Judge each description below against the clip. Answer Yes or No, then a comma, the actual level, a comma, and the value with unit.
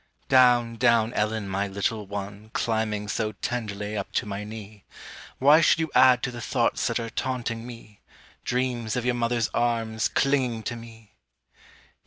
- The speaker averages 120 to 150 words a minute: No, average, 160 wpm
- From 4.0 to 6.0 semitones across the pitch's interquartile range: No, narrow, 2.4 semitones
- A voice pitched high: No, low, 115 Hz